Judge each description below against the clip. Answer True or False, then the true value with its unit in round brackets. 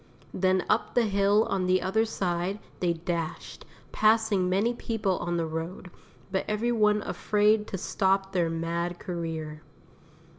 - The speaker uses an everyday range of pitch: True (3.4 semitones)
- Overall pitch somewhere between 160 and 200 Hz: True (190 Hz)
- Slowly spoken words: False (145 wpm)